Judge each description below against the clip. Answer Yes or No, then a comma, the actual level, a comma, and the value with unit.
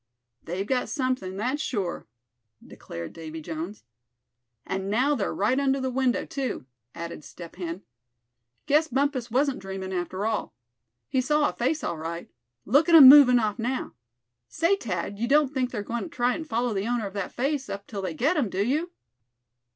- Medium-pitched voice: No, high, 240 Hz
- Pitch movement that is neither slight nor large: No, wide, 6.1 semitones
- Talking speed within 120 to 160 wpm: No, average, 180 wpm